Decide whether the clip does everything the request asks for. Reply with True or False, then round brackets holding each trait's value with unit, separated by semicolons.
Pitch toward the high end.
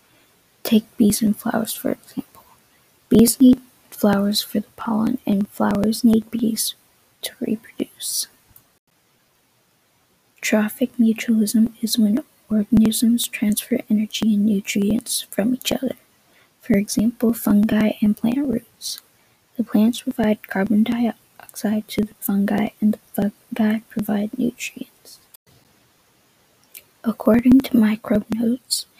True (225 Hz)